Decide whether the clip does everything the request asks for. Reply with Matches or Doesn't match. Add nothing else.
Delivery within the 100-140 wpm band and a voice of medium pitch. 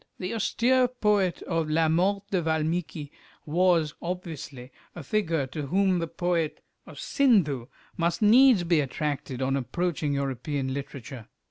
Matches